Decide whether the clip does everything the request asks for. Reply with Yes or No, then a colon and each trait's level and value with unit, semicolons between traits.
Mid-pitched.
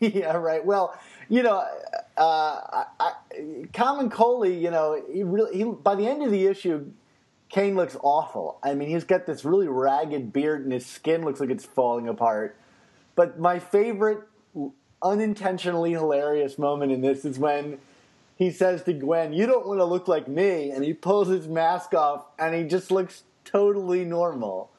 Yes: medium, 175 Hz